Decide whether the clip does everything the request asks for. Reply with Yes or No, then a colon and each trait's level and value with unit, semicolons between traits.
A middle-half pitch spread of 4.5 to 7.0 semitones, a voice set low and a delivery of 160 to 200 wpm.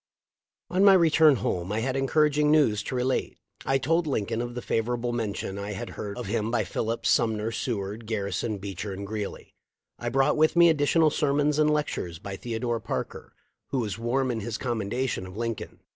Yes: average, 5.1 semitones; low, 120 Hz; average, 190 wpm